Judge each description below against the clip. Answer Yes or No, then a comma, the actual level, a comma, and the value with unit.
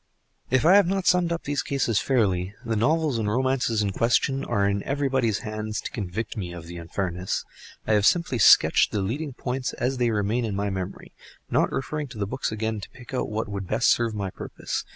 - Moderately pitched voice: No, low, 110 Hz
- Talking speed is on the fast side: Yes, fast, 215 wpm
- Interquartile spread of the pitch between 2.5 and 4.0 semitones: No, average, 4.8 semitones